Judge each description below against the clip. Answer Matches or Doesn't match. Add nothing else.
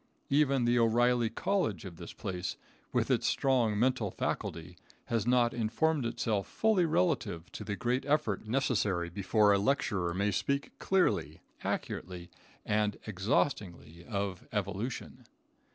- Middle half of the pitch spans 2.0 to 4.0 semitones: Doesn't match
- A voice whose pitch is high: Doesn't match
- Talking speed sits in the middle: Doesn't match